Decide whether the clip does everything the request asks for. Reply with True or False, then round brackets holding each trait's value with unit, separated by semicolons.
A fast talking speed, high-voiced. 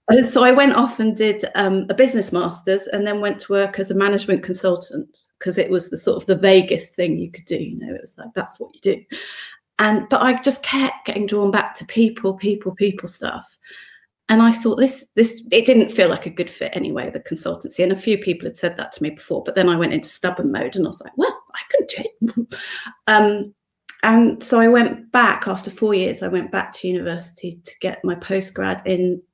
True (235 wpm; 205 Hz)